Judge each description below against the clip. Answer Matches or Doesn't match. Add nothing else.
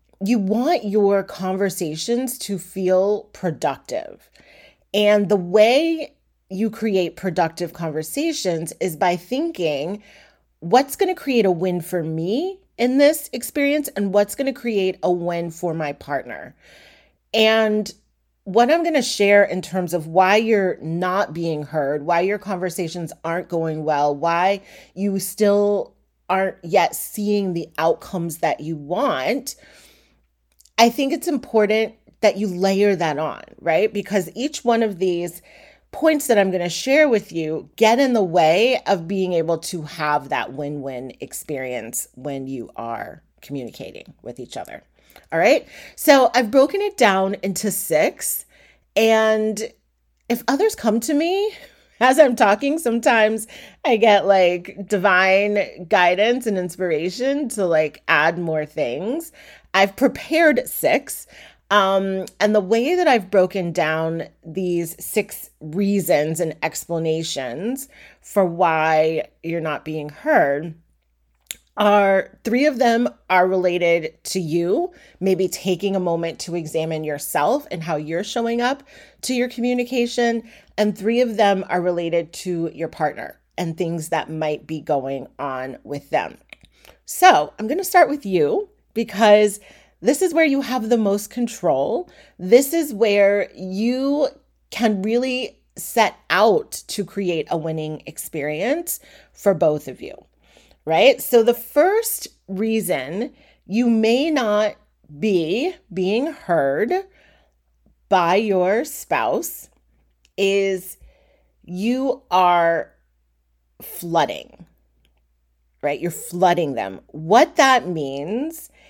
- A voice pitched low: Doesn't match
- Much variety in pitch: Matches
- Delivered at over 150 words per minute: Doesn't match